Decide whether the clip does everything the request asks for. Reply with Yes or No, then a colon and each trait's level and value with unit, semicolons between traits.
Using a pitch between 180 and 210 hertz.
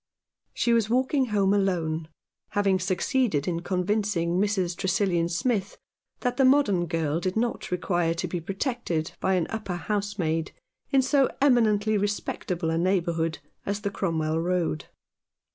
Yes: high, 190 Hz